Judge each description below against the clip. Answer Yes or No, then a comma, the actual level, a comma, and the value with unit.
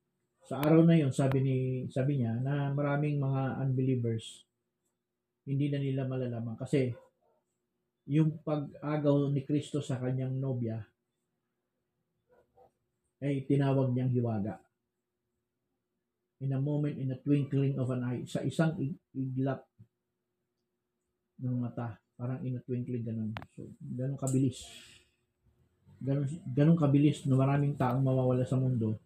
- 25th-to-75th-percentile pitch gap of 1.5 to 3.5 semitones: Yes, narrow, 2.5 semitones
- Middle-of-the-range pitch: No, low, 130 Hz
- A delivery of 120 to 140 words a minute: Yes, average, 130 wpm